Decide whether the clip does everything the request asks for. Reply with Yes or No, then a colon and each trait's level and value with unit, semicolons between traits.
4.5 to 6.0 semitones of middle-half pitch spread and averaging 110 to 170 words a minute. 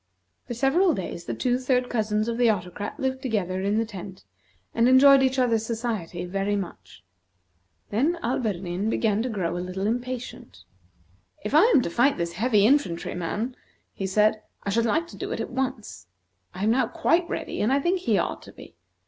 No: average, 5.1 semitones; average, 190 wpm